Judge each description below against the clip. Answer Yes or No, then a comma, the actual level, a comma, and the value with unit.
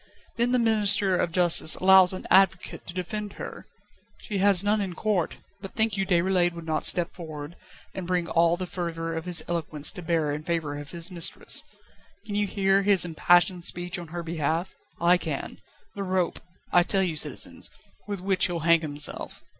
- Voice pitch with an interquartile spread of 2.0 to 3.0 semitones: Yes, narrow, 2.5 semitones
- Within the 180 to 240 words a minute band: Yes, average, 185 wpm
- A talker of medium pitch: Yes, medium, 175 Hz